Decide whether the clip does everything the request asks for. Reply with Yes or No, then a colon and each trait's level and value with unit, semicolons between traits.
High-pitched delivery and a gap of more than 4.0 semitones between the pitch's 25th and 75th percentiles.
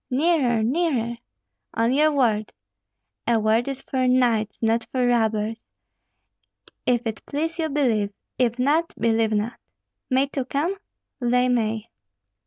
No: high, 245 Hz; average, 3.5 semitones